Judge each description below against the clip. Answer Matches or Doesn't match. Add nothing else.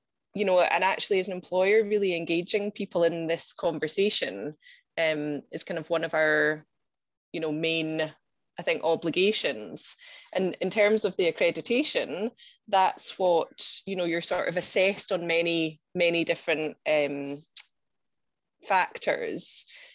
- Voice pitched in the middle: Matches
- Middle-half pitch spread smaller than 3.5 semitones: Doesn't match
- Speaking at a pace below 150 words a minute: Matches